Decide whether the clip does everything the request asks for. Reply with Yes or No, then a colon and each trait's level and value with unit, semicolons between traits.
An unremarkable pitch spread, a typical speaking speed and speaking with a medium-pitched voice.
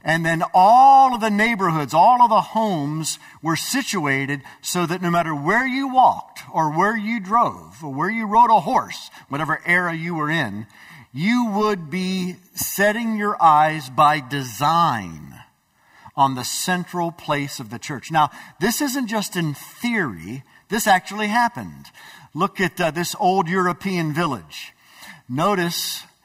No: wide, 5.8 semitones; average, 150 wpm; medium, 175 Hz